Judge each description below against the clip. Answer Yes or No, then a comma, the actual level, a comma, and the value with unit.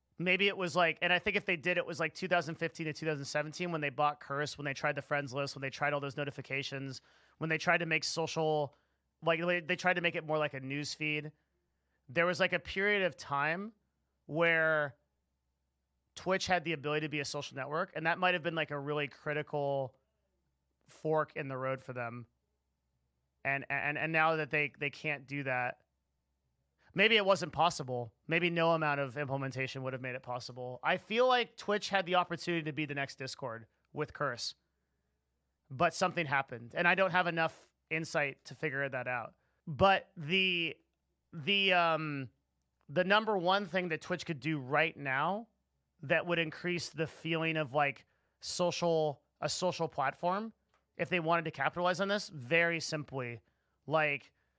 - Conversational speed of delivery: Yes, average, 180 wpm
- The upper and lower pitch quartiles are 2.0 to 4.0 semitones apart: No, average, 4.5 semitones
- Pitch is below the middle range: No, medium, 150 Hz